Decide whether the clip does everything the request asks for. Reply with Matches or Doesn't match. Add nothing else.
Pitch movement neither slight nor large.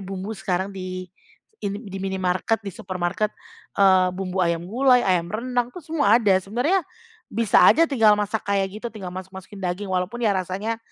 Matches